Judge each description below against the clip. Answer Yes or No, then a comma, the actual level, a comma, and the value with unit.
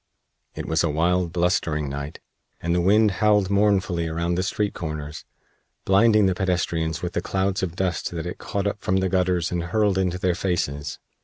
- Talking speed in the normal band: Yes, average, 185 wpm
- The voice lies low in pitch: Yes, very low, 90 Hz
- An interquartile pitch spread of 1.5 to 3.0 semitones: Yes, narrow, 2.4 semitones